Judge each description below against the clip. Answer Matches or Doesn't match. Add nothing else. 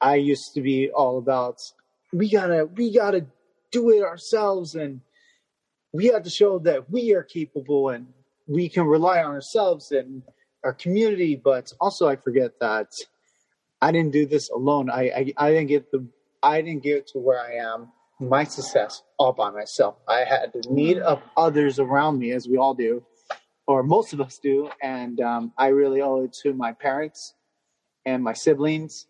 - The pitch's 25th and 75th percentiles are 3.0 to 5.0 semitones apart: Matches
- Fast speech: Doesn't match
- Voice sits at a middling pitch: Matches